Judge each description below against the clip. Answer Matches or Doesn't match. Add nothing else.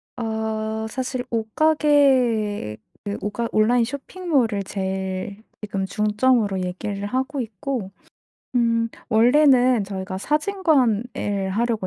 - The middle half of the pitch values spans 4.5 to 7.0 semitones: Doesn't match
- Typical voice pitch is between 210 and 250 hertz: Matches